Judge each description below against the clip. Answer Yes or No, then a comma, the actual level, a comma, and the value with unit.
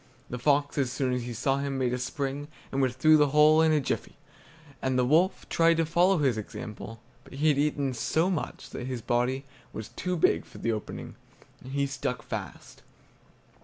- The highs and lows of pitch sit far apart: No, average, 3.4 semitones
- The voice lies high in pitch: No, medium, 140 Hz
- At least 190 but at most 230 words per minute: Yes, average, 200 wpm